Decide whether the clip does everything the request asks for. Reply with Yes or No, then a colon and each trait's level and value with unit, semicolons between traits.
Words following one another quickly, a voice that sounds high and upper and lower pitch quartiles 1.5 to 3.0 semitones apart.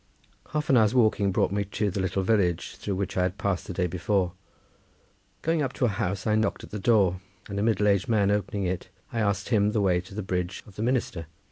No: fast, 240 wpm; low, 100 Hz; average, 2.7 semitones